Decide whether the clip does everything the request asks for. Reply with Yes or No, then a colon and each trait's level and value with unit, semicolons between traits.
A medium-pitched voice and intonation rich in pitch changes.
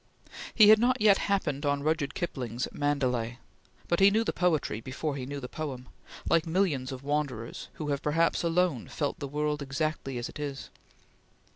No: medium, 145 Hz; average, 3.8 semitones